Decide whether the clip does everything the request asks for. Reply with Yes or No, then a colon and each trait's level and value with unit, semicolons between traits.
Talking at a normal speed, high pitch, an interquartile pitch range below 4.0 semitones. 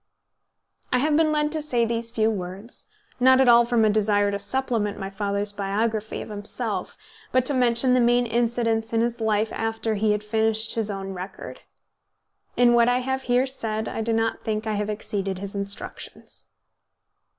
Yes: average, 185 wpm; high, 225 Hz; average, 2.7 semitones